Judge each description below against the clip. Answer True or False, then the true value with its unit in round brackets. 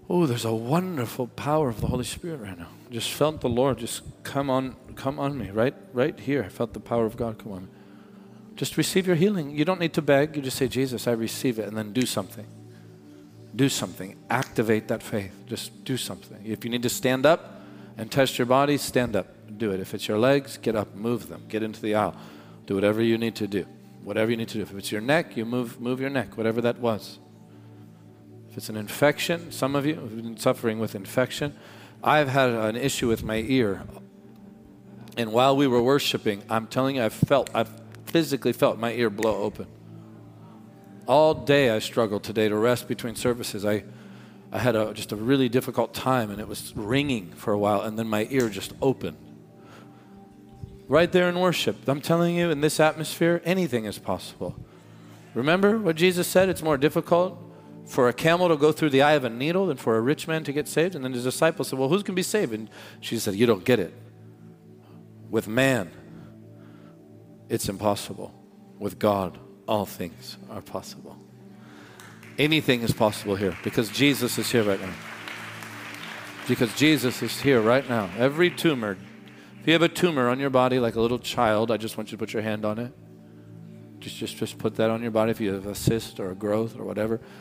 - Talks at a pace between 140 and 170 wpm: False (205 wpm)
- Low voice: True (120 Hz)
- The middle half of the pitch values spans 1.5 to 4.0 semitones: False (4.5 semitones)